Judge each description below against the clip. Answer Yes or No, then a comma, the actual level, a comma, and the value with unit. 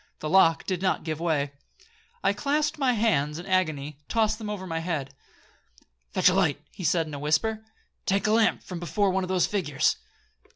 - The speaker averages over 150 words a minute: Yes, average, 190 wpm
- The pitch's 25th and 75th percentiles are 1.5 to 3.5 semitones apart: No, wide, 5.4 semitones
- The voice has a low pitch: No, medium, 185 Hz